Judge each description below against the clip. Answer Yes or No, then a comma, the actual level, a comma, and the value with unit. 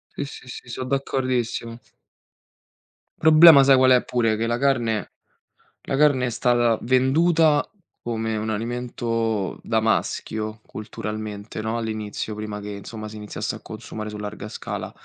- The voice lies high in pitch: No, low, 115 Hz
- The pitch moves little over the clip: No, average, 3.1 semitones